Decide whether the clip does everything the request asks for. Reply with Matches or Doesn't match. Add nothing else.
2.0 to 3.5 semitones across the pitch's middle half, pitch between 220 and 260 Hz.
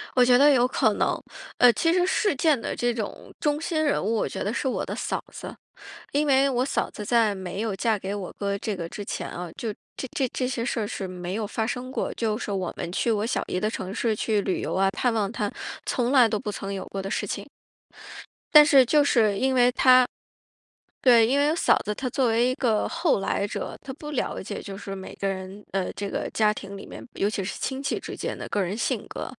Doesn't match